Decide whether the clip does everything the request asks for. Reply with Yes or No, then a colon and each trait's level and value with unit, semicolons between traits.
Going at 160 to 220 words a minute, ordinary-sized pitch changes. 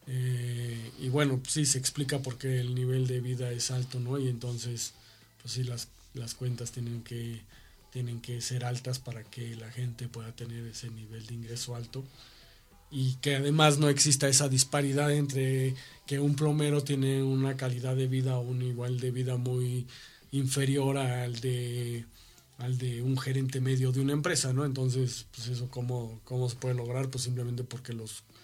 No: average, 180 wpm; narrow, 1.8 semitones